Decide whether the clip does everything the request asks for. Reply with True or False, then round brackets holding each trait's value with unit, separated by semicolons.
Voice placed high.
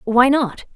True (250 Hz)